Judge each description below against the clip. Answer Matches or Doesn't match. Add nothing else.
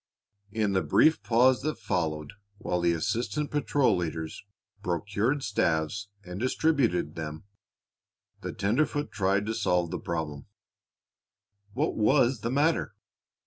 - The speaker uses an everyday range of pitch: Doesn't match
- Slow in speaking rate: Matches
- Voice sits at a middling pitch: Doesn't match